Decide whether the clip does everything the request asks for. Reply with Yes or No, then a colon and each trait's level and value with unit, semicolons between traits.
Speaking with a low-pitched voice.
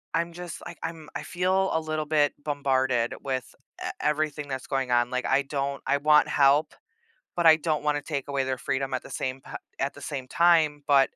No: medium, 145 Hz